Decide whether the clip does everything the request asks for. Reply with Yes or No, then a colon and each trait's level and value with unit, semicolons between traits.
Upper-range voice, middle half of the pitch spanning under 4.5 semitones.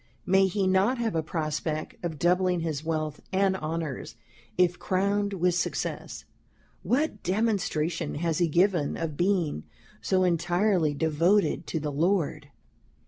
No: medium, 175 Hz; average, 3.4 semitones